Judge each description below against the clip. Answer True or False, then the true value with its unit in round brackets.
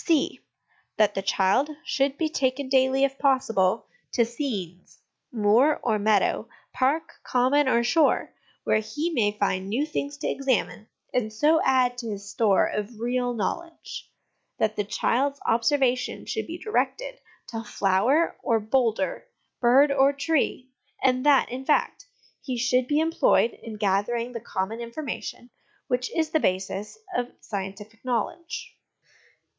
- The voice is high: True (250 Hz)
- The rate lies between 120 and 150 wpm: True (140 wpm)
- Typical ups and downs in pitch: True (4.5 semitones)